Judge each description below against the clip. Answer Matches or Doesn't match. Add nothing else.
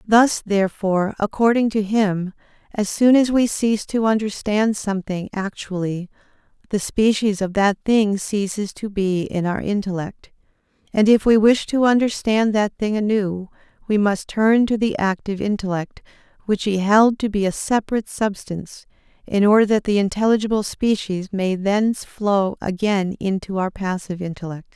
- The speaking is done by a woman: Matches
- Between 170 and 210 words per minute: Doesn't match